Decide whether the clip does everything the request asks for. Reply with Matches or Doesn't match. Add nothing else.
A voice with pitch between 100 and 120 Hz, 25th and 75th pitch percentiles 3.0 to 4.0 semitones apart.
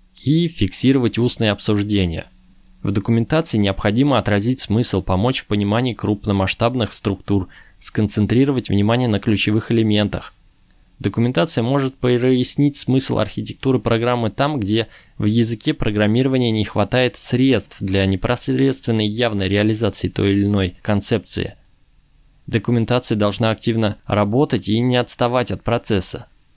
Matches